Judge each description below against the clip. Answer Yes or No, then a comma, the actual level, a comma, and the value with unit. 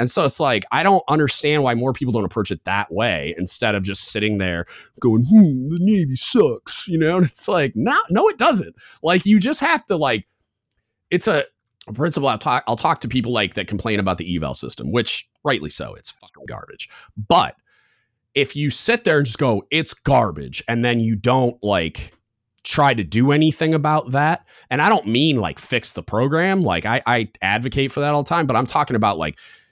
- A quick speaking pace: Yes, fast, 215 wpm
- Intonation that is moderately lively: No, wide, 6.3 semitones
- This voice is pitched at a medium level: No, low, 130 Hz